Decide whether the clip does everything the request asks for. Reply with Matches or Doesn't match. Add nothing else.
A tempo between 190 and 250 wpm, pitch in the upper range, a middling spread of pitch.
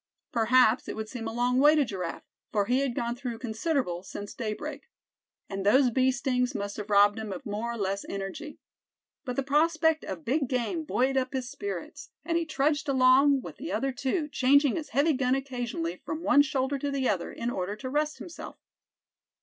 Matches